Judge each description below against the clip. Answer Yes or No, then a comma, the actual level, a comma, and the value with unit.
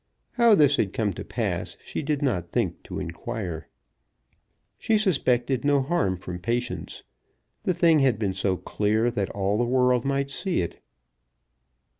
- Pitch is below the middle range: Yes, low, 120 Hz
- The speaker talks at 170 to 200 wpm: No, average, 155 wpm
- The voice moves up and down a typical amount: No, wide, 6.1 semitones